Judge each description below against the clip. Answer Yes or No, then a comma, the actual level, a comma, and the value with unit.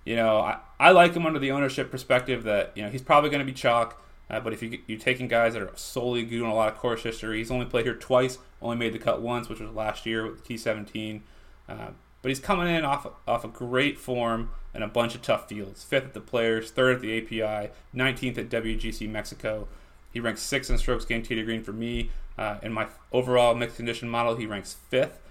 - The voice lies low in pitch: Yes, low, 115 Hz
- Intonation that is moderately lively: No, narrow, 2.3 semitones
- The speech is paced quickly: Yes, fast, 240 wpm